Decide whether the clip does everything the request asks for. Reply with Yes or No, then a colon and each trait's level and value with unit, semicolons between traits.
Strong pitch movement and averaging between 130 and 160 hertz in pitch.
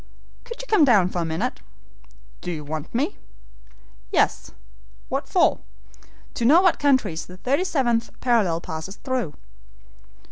No: wide, 8.7 semitones; high, 230 Hz